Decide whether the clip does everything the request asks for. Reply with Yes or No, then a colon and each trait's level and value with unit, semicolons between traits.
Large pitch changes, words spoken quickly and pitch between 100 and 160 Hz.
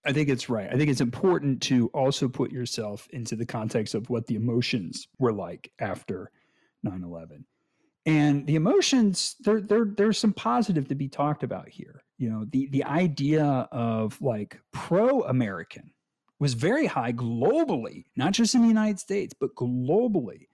No: wide, 7.9 semitones; average, 165 wpm; medium, 140 Hz